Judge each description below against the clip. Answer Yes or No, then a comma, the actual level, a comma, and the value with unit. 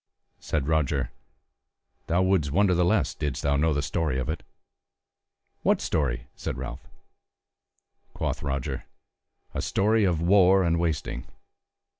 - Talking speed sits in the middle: No, slow, 130 wpm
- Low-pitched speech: Yes, very low, 80 Hz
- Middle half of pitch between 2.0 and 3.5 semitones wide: No, average, 4.6 semitones